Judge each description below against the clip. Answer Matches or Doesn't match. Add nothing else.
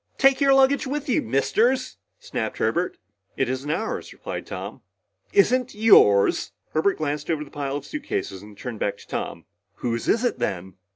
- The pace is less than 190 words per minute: Matches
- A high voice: Doesn't match